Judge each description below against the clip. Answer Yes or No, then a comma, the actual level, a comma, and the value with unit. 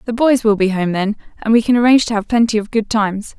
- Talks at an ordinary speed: No, fast, 285 wpm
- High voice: Yes, high, 220 Hz